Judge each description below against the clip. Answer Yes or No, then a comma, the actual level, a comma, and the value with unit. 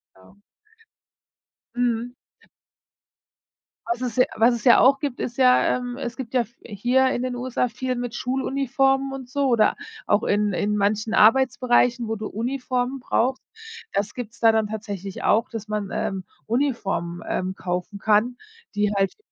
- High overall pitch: Yes, high, 235 Hz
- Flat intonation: No, average, 3.3 semitones